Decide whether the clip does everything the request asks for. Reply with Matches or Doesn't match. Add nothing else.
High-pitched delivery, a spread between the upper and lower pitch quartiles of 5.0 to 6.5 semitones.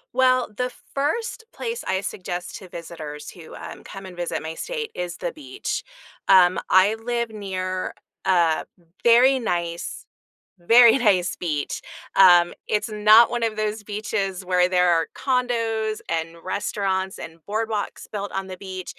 Doesn't match